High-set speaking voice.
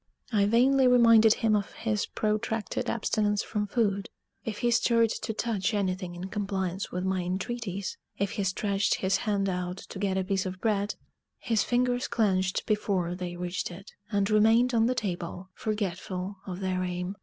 Yes: high, 200 Hz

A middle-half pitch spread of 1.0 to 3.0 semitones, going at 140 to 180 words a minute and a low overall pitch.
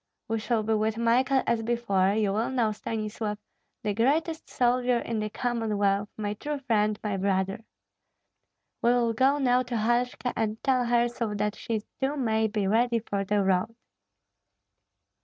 No: average, 2.7 semitones; average, 160 wpm; high, 225 Hz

